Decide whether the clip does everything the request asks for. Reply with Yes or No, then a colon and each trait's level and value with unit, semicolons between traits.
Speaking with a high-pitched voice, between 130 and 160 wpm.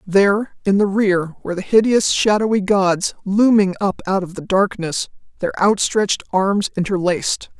Yes: high, 195 Hz; average, 150 wpm